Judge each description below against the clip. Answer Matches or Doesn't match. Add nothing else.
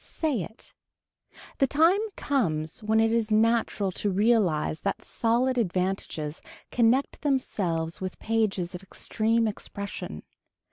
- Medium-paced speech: Doesn't match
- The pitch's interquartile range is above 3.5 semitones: Matches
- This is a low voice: Doesn't match